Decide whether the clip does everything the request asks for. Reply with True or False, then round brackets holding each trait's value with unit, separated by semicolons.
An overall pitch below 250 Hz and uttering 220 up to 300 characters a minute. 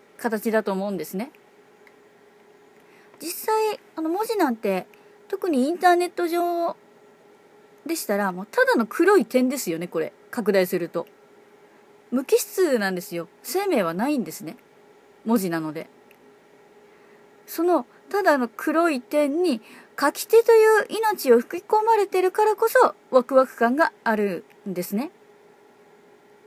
False (300 Hz; 255 characters per minute)